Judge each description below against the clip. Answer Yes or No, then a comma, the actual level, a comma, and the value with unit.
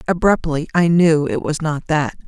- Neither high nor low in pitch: Yes, medium, 155 Hz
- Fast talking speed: No, average, 185 wpm